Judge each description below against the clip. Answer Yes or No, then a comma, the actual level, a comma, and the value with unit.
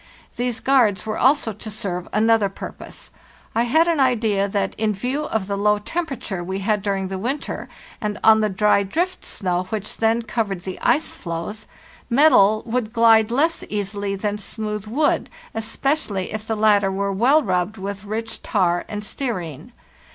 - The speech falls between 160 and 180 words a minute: Yes, average, 165 wpm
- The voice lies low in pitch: No, high, 215 Hz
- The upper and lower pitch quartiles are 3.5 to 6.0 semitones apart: No, average, 3.0 semitones